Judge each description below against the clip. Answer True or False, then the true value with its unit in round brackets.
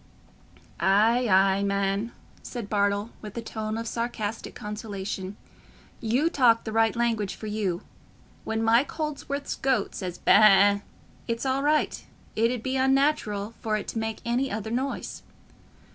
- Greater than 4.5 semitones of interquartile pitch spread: False (3.1 semitones)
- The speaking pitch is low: False (225 Hz)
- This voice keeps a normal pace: True (145 wpm)